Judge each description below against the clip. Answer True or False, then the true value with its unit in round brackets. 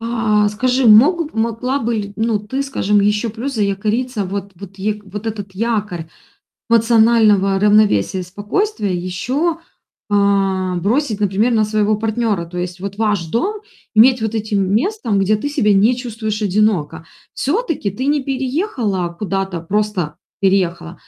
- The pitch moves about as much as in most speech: True (3.2 semitones)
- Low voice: False (210 Hz)